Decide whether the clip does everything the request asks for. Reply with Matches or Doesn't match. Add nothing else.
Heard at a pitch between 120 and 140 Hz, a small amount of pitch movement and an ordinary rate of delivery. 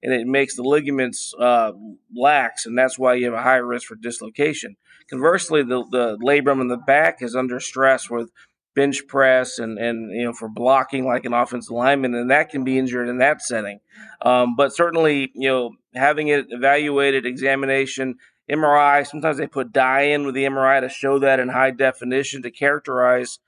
Matches